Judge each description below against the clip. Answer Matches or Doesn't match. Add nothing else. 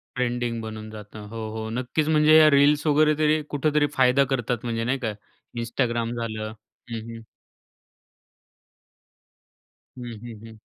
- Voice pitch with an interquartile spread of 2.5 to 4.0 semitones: Doesn't match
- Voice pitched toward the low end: Matches